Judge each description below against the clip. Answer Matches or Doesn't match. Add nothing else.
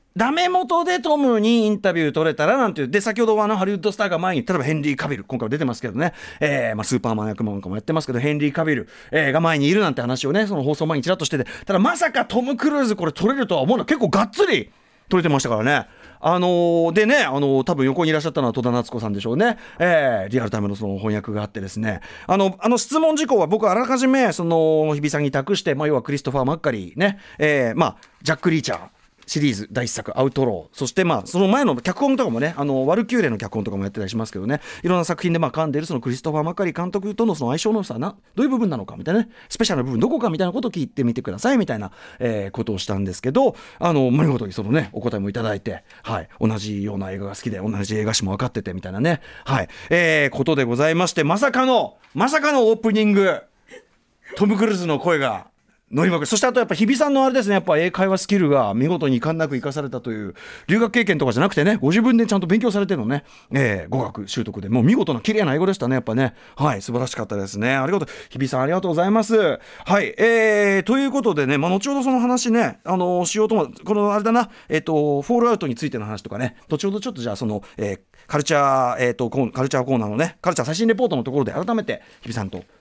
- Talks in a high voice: Doesn't match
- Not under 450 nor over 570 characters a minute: Matches